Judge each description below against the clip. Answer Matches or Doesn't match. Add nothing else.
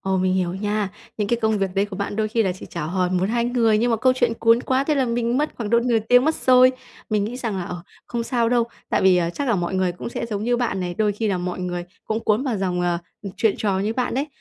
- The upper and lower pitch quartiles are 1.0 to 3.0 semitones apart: Doesn't match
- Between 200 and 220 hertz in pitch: Matches